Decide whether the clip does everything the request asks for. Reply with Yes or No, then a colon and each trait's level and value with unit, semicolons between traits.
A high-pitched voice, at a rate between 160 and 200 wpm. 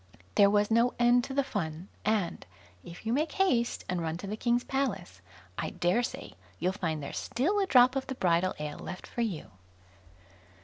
Yes: high, 220 Hz; average, 190 wpm